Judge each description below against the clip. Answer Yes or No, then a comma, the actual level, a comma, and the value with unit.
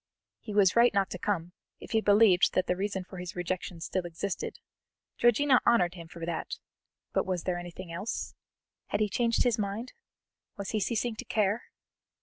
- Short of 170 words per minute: No, average, 180 wpm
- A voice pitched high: Yes, high, 195 Hz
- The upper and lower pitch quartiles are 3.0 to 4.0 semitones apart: Yes, average, 3.6 semitones